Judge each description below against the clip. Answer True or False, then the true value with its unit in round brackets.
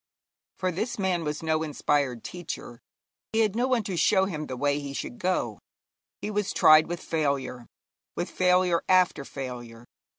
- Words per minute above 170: False (165 wpm)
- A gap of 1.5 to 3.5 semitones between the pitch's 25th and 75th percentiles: False (4.7 semitones)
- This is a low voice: False (165 Hz)